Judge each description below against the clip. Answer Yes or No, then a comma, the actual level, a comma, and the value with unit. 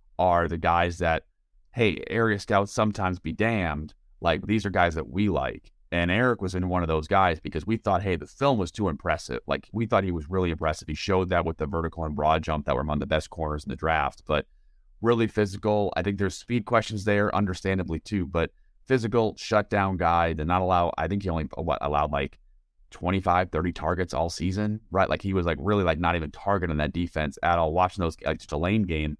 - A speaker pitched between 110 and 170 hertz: No, very low, 90 Hz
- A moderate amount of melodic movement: Yes, average, 4.0 semitones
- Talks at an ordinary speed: No, fast, 225 wpm